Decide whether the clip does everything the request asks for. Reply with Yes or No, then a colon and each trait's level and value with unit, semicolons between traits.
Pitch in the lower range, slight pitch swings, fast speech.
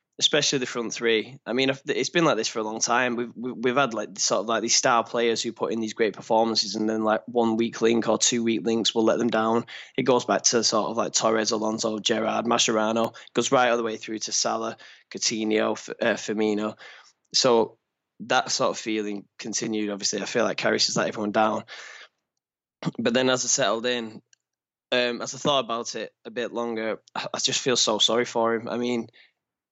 Yes: low, 115 Hz; narrow, 1.6 semitones; fast, 215 wpm